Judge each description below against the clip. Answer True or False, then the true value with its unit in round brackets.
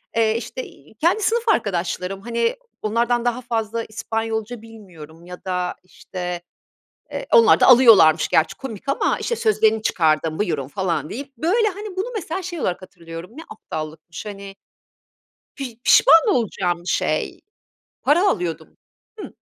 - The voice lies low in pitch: False (220 Hz)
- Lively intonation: True (7.0 semitones)